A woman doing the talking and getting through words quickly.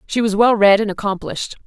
Yes: female; fast, 215 wpm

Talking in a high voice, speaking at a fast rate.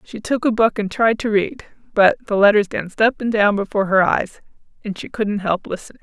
Yes: high, 210 Hz; fast, 230 wpm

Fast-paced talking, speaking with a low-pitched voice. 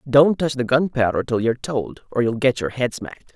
Yes: fast, 230 wpm; low, 130 Hz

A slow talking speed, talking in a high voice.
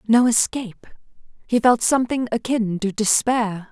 Yes: slow, 130 wpm; high, 230 Hz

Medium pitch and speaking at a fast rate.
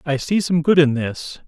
Yes: medium, 155 Hz; fast, 245 wpm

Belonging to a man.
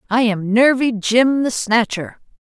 No: female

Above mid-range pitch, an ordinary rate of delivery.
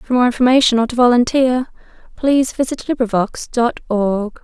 Yes: high, 245 Hz; average, 150 wpm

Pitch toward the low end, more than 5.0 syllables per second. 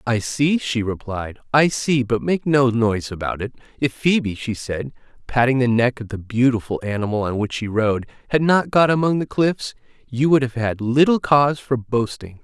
No: low, 125 Hz; 4.9 syllables/s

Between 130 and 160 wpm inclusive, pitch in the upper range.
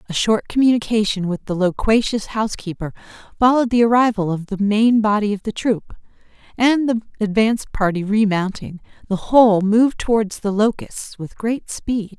Yes: average, 155 wpm; high, 215 Hz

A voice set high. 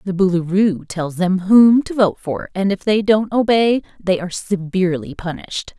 Yes: high, 195 Hz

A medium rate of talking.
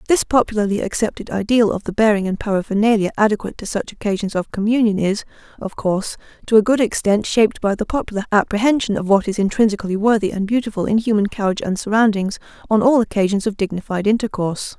Yes: average, 185 wpm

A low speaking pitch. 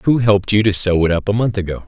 Yes: low, 100 Hz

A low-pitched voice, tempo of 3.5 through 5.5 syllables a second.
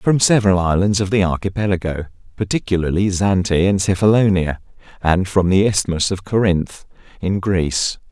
Yes: very low, 95 Hz; 5.2 syllables/s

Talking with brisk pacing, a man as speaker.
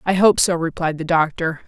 No: fast, 215 wpm; female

